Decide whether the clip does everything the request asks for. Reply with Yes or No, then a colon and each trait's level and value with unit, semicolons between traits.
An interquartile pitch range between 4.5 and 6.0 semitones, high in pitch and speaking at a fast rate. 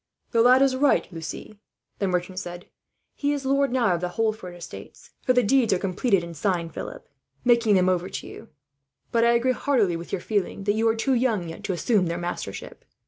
Yes: wide, 5.6 semitones; high, 210 Hz; fast, 210 wpm